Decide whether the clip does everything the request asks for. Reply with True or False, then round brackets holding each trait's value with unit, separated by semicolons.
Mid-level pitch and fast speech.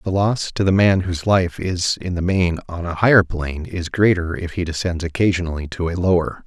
False (90 Hz; 225 wpm)